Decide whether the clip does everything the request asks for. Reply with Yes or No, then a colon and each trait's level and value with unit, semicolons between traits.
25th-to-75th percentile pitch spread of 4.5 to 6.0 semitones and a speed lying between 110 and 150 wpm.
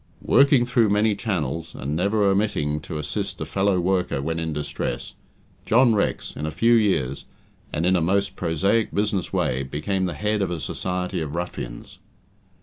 No: average, 5.2 semitones; average, 170 wpm